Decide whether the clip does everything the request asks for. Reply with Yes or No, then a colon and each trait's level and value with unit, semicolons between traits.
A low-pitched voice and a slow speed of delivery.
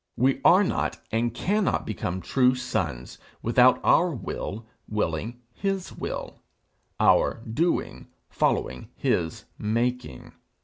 Yes: low, 120 Hz; slow, 105 wpm